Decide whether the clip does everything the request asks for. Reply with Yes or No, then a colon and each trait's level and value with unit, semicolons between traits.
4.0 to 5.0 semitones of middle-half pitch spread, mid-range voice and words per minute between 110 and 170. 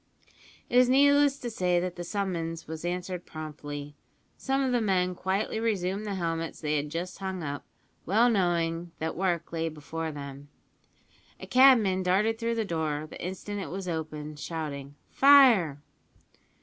Yes: average, 4.6 semitones; medium, 180 Hz; average, 160 wpm